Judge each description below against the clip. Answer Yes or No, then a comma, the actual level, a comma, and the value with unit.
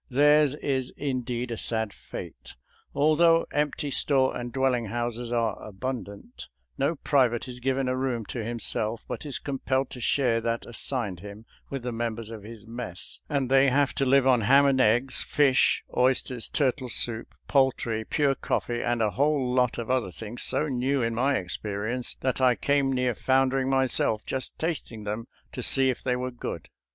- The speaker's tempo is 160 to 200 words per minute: Yes, average, 180 wpm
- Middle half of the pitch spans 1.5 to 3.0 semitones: Yes, average, 2.7 semitones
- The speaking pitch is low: Yes, low, 125 Hz